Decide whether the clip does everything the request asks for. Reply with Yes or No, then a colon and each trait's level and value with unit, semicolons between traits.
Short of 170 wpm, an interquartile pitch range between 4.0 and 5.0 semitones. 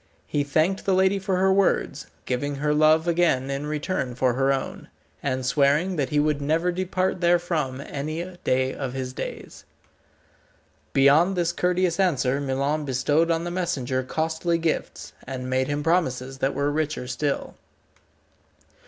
Yes: average, 155 wpm; average, 4.4 semitones